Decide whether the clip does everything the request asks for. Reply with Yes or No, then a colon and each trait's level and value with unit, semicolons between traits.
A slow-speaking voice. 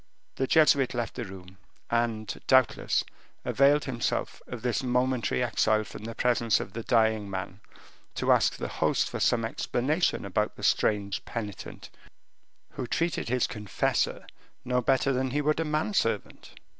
No: average, 155 wpm